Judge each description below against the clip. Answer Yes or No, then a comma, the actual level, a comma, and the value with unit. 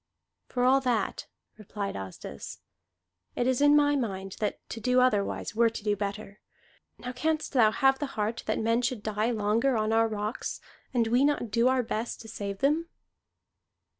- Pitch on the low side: No, high, 230 Hz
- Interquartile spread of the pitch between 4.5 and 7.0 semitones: No, average, 3.4 semitones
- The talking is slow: No, average, 175 wpm